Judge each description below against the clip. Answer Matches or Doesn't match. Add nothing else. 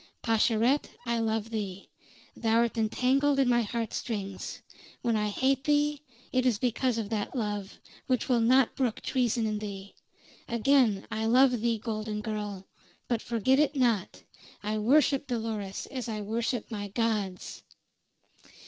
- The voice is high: Matches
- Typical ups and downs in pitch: Matches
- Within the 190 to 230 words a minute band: Doesn't match